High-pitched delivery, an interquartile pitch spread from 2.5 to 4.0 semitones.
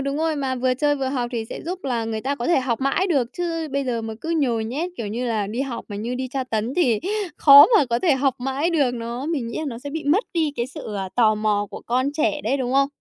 Yes: very high, 260 Hz; average, 3.7 semitones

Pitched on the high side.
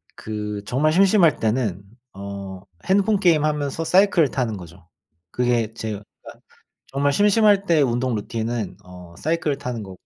No: low, 125 Hz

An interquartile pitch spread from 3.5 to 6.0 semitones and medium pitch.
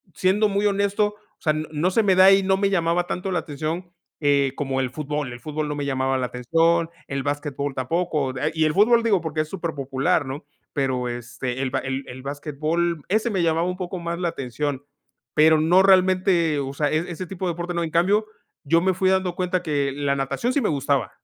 Yes: average, 4.6 semitones; medium, 160 Hz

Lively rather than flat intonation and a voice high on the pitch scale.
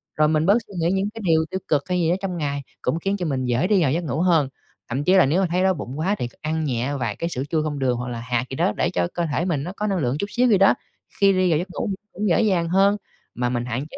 No: wide, 5.8 semitones; medium, 160 Hz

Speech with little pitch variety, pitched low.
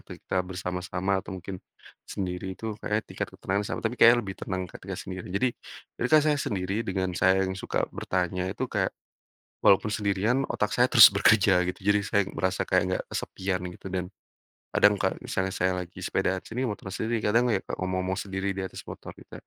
Yes: narrow, 2.0 semitones; very low, 95 Hz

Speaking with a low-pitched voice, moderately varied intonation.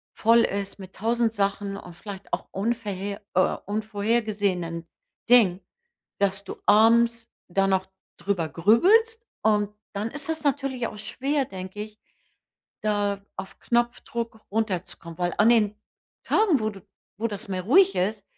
No: high, 210 Hz; average, 3.1 semitones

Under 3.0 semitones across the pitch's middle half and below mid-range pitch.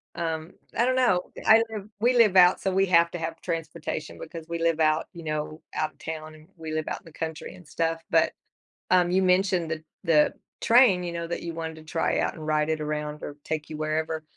No: narrow, 2.4 semitones; medium, 165 Hz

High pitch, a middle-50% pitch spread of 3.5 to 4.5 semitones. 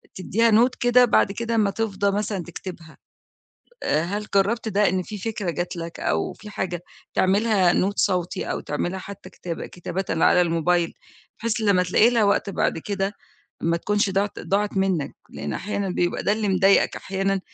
No: high, 195 Hz; average, 2.8 semitones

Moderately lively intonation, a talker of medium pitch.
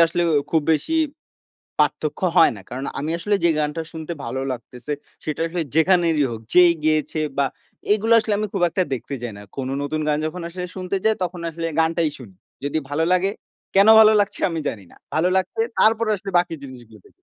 Yes: average, 4.1 semitones; medium, 165 Hz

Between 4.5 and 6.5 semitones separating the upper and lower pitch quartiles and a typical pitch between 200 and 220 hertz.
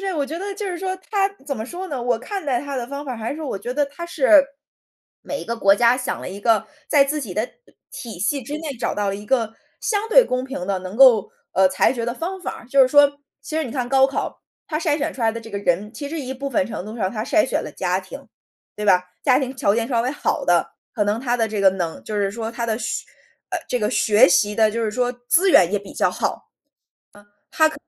No: average, 5.2 semitones; very high, 250 Hz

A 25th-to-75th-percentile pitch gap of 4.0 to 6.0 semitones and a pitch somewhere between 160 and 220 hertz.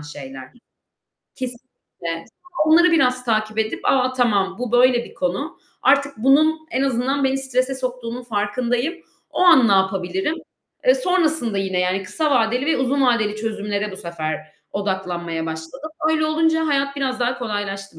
No: wide, 5.6 semitones; high, 245 Hz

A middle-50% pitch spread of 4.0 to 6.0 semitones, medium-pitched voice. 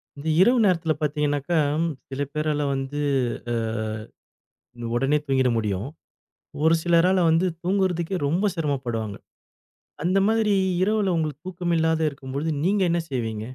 Yes: average, 4.8 semitones; medium, 160 Hz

